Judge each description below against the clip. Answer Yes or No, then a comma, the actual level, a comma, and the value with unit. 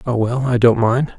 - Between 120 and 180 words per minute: No, fast, 205 wpm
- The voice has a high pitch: No, low, 120 Hz